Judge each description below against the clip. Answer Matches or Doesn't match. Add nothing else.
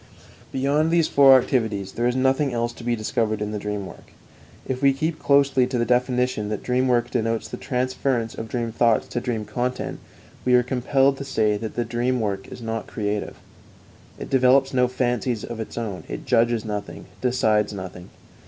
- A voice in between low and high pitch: Doesn't match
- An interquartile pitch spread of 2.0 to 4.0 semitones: Matches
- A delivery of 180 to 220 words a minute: Matches